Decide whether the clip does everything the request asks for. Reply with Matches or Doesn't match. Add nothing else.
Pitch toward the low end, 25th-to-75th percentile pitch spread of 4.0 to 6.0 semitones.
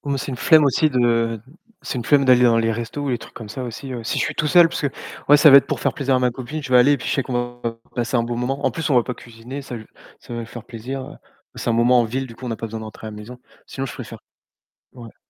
Doesn't match